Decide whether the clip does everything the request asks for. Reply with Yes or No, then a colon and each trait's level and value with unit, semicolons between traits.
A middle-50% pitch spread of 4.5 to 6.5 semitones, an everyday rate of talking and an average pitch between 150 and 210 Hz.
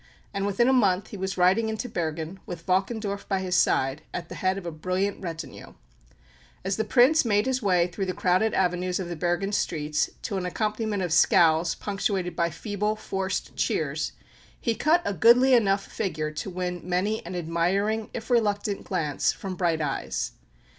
No: average, 3.3 semitones; average, 180 wpm; high, 190 Hz